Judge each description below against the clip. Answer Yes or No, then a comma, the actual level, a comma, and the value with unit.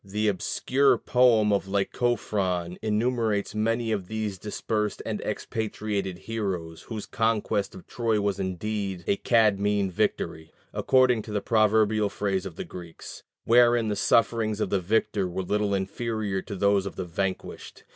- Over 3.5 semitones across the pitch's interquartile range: No, narrow, 2.4 semitones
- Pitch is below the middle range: Yes, low, 105 Hz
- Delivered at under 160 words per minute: Yes, average, 145 wpm